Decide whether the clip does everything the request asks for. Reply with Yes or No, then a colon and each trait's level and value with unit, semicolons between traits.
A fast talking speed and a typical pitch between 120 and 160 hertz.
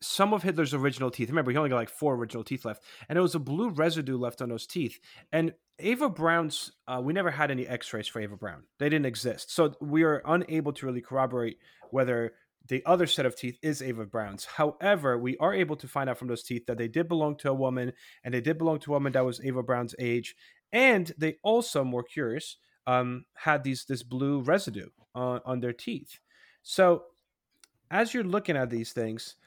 Yes: fast, 215 wpm; low, 135 Hz